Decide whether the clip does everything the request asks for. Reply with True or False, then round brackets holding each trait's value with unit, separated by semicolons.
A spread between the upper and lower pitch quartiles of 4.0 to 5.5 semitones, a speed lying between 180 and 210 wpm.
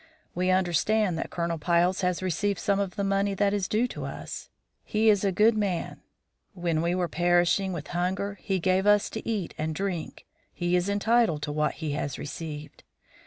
False (2.9 semitones; 190 wpm)